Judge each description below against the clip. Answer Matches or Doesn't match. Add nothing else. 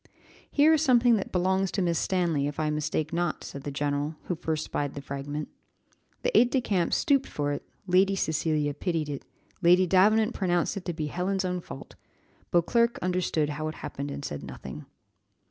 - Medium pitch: Matches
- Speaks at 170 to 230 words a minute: Matches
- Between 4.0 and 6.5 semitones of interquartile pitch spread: Matches